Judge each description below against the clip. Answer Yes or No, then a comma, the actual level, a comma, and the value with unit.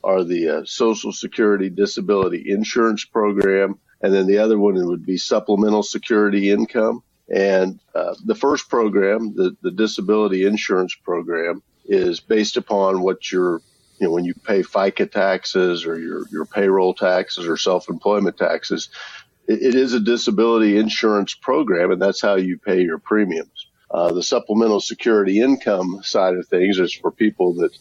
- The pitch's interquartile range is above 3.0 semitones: No, narrow, 2.4 semitones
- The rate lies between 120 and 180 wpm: Yes, average, 160 wpm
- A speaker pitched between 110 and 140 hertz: No, low, 100 Hz